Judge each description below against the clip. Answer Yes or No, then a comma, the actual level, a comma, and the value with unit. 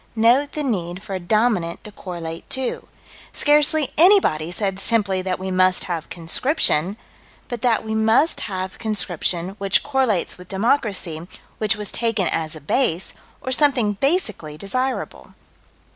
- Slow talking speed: No, average, 145 wpm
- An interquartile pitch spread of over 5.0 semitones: Yes, wide, 5.5 semitones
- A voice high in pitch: Yes, high, 205 Hz